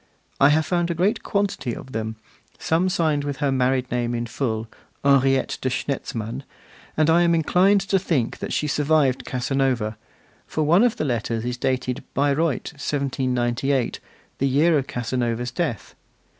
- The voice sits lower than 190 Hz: Yes, low, 135 Hz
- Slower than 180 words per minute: Yes, average, 155 wpm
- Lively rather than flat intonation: No, average, 4.3 semitones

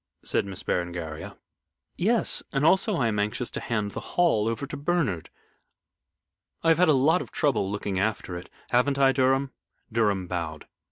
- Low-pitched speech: Yes, low, 115 Hz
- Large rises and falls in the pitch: Yes, wide, 6.8 semitones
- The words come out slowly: No, average, 175 wpm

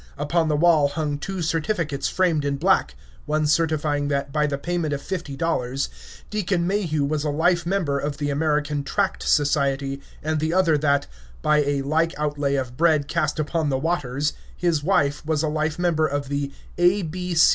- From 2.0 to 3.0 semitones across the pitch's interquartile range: Yes, narrow, 2.6 semitones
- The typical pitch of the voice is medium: Yes, medium, 150 Hz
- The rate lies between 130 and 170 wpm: No, average, 180 wpm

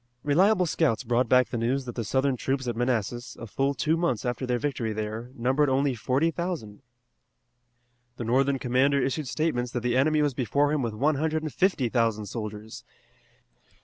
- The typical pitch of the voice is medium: No, low, 130 Hz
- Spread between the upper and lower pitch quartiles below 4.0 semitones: Yes, average, 3.6 semitones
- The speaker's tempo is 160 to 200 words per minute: Yes, average, 180 wpm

